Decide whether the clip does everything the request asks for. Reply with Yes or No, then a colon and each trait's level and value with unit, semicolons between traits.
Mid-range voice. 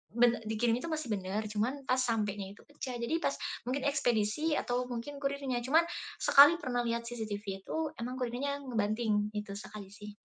No: high, 240 Hz